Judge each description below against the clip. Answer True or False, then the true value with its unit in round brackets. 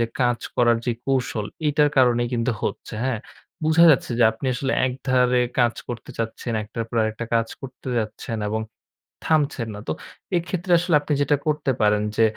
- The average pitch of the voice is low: True (125 Hz)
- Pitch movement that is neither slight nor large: True (3.4 semitones)